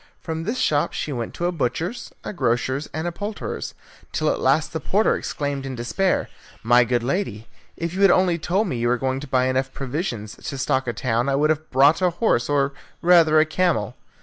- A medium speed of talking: No, fast, 215 wpm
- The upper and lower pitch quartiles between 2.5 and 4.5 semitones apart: No, wide, 5.5 semitones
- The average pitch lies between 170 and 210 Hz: No, medium, 145 Hz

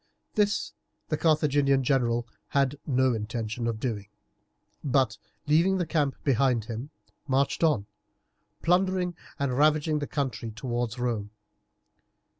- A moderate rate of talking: No, slow, 115 wpm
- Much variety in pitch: No, average, 4.3 semitones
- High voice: No, low, 135 Hz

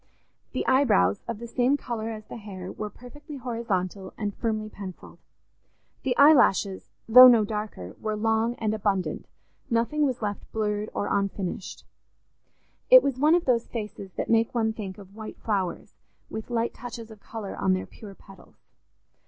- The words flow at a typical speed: Yes, average, 160 wpm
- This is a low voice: No, high, 220 Hz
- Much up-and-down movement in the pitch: No, average, 3.0 semitones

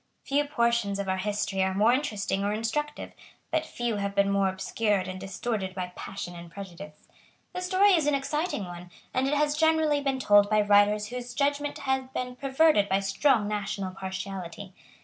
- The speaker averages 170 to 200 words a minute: Yes, average, 180 wpm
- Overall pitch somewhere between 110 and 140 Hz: No, high, 210 Hz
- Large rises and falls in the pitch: Yes, wide, 6.1 semitones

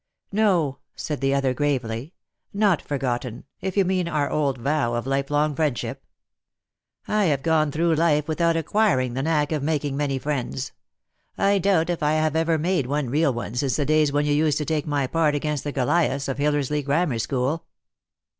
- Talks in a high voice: No, medium, 150 Hz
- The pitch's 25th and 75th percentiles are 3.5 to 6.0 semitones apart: No, average, 3.0 semitones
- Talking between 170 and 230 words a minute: Yes, average, 190 wpm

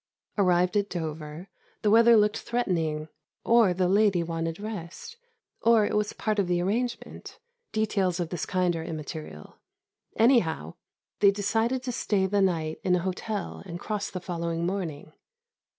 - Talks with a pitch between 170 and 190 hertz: Yes, medium, 185 Hz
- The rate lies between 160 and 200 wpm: No, average, 150 wpm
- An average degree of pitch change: Yes, average, 4.0 semitones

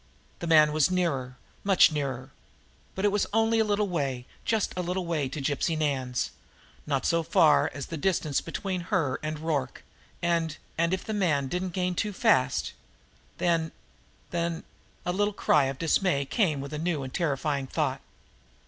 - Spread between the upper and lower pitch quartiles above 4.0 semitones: Yes, average, 4.6 semitones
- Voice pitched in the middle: Yes, medium, 165 Hz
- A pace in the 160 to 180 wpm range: Yes, average, 170 wpm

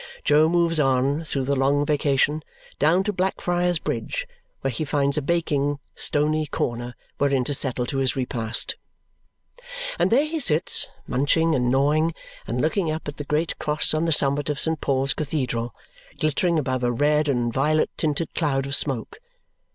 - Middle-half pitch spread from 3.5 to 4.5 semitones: No, average, 2.8 semitones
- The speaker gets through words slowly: No, average, 165 wpm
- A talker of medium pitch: Yes, medium, 145 Hz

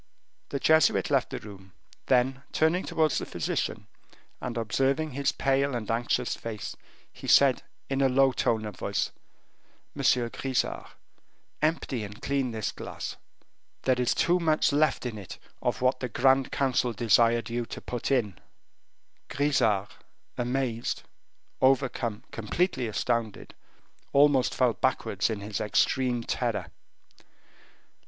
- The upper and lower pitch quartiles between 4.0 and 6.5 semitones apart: No, average, 3.1 semitones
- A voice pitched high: No, low, 125 Hz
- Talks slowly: Yes, slow, 130 wpm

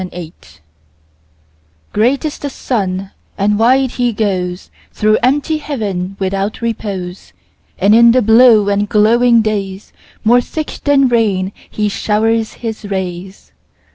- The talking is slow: Yes, slow, 120 wpm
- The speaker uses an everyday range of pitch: Yes, average, 3.6 semitones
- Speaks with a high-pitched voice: Yes, high, 215 Hz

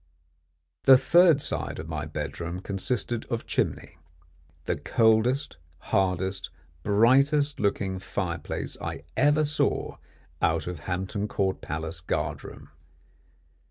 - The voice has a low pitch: Yes, low, 100 Hz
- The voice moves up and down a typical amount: No, wide, 6.2 semitones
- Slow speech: Yes, slow, 110 wpm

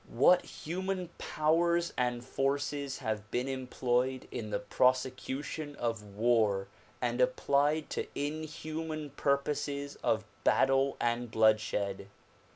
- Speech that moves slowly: Yes, slow, 105 wpm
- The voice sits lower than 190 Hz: Yes, low, 135 Hz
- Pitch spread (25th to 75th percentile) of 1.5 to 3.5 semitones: No, average, 4.3 semitones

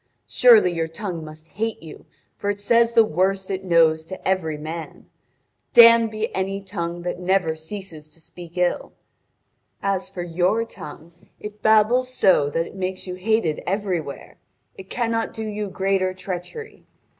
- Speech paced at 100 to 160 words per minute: Yes, average, 155 wpm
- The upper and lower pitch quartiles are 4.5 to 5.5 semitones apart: No, average, 4.0 semitones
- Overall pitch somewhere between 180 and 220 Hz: Yes, high, 190 Hz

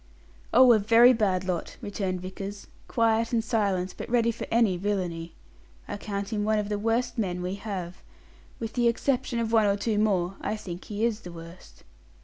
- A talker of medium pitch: No, high, 210 Hz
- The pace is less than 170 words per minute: No, average, 190 wpm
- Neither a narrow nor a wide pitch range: Yes, average, 3.6 semitones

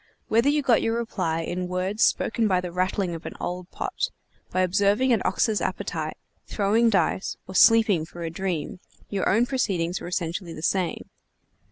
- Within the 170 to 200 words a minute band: Yes, average, 175 wpm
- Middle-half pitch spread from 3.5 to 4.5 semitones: Yes, average, 4.1 semitones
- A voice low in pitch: No, high, 190 Hz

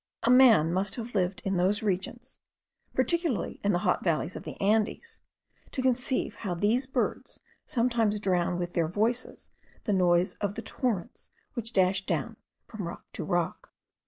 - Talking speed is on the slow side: No, average, 160 wpm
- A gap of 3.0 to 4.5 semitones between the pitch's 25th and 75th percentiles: No, average, 4.9 semitones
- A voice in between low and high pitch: No, high, 205 Hz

